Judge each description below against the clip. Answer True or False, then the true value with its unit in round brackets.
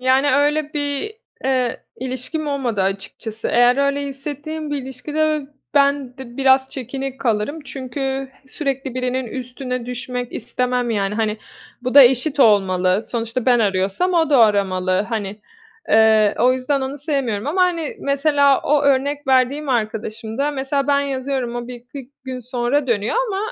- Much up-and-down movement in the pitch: False (3.1 semitones)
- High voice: True (260 Hz)